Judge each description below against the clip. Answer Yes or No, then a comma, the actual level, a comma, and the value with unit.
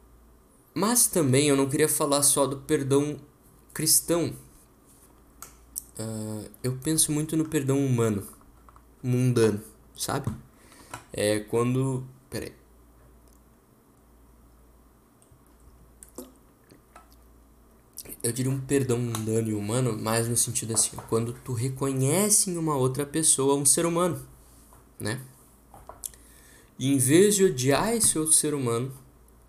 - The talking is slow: Yes, slow, 110 wpm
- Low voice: Yes, low, 125 Hz